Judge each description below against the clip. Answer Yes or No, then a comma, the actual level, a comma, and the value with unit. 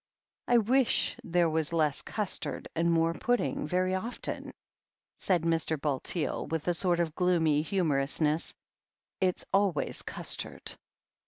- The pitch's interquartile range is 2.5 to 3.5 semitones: Yes, average, 2.9 semitones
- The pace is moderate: No, slow, 120 wpm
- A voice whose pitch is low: No, medium, 170 Hz